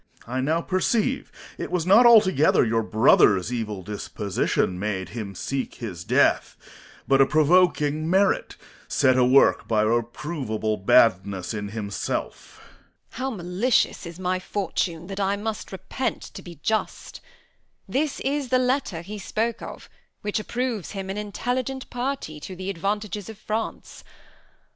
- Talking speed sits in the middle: Yes, average, 145 wpm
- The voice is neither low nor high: Yes, medium, 180 Hz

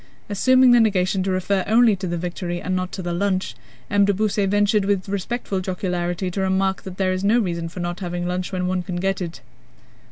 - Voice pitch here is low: No, high, 190 Hz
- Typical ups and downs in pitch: No, narrow, 2.0 semitones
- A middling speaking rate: No, fast, 220 wpm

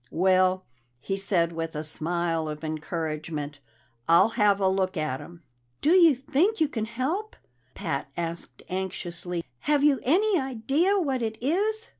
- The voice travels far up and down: Yes, wide, 9.0 semitones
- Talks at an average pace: Yes, average, 150 wpm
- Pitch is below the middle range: No, high, 190 Hz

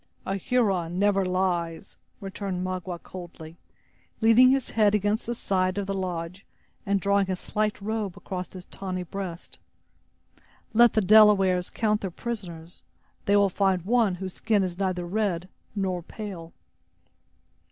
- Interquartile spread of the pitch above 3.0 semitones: No, narrow, 2.4 semitones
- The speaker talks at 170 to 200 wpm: No, average, 140 wpm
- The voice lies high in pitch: Yes, high, 195 Hz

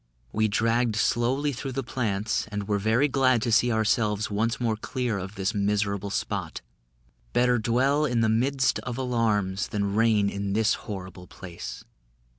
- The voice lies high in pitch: No, low, 110 Hz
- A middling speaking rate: Yes, average, 160 wpm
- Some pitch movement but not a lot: Yes, average, 3.2 semitones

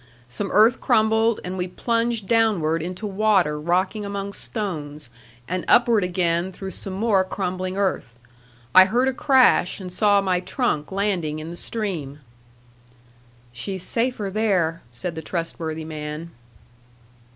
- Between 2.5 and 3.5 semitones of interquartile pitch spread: No, average, 4.2 semitones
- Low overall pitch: No, medium, 185 Hz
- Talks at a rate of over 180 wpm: No, slow, 135 wpm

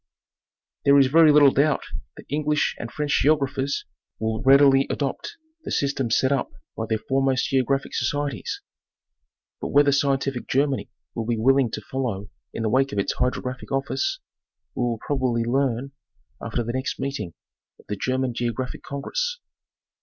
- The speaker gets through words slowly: No, average, 155 wpm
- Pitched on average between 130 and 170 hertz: Yes, low, 135 Hz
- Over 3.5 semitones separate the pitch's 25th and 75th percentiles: No, average, 2.7 semitones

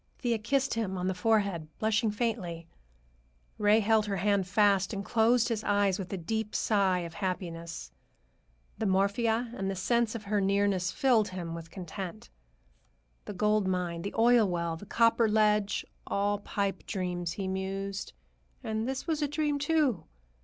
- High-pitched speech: Yes, high, 205 Hz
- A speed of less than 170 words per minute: Yes, average, 160 wpm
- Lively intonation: No, average, 3.0 semitones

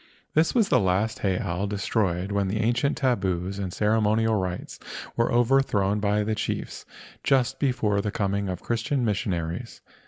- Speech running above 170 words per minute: No, average, 150 wpm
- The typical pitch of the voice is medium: No, low, 105 Hz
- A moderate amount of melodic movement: Yes, average, 3.5 semitones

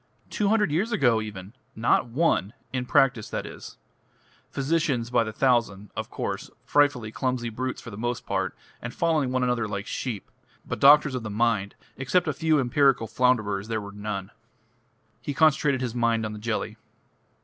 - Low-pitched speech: Yes, low, 120 Hz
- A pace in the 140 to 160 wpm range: No, average, 170 wpm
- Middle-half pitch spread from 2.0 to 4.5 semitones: Yes, average, 4.2 semitones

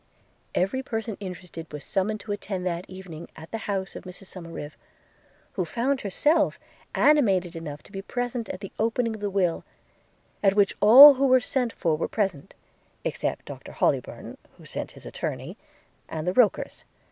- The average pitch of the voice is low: No, high, 195 Hz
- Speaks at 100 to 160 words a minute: No, average, 170 wpm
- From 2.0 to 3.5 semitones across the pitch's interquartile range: No, average, 4.3 semitones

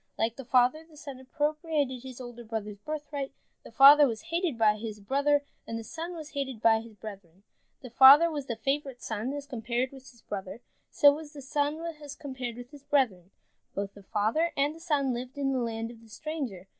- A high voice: Yes, very high, 260 Hz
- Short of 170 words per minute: No, fast, 205 wpm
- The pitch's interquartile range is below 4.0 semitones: No, average, 4.3 semitones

